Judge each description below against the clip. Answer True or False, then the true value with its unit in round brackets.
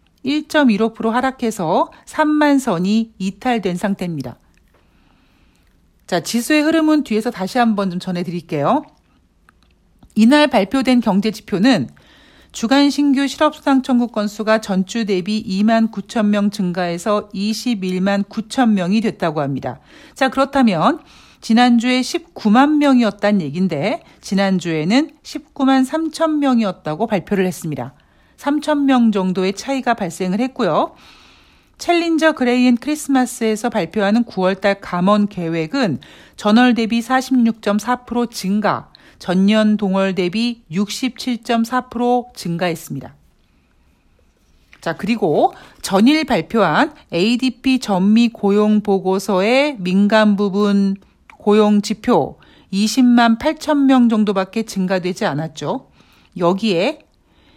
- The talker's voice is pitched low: False (215 Hz)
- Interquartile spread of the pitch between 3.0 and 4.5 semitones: False (4.9 semitones)